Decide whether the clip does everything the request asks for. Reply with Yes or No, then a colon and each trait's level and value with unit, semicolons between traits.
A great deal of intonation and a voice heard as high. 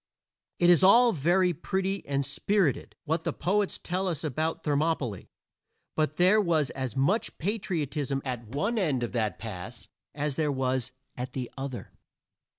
No: wide, 5.7 semitones; medium, 150 Hz